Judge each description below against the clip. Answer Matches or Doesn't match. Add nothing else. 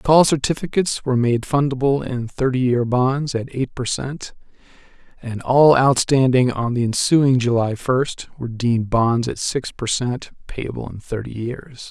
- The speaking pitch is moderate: Doesn't match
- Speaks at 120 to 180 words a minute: Matches